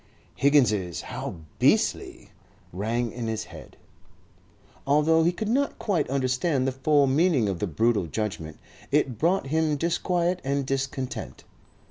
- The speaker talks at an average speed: No, slow, 130 wpm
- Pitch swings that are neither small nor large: No, wide, 6.0 semitones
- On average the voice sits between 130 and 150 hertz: Yes, low, 135 Hz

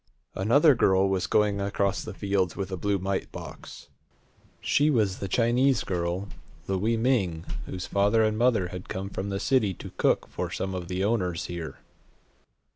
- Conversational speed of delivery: Yes, average, 170 wpm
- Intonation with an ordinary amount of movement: Yes, average, 3.0 semitones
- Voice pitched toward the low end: Yes, low, 100 Hz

